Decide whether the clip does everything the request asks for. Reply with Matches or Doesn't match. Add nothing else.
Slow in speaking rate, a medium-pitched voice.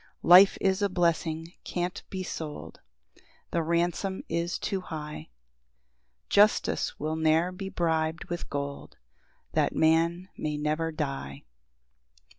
Matches